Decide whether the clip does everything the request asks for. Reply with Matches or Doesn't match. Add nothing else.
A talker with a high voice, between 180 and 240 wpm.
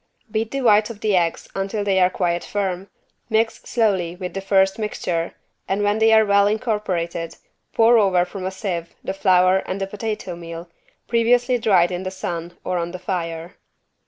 Matches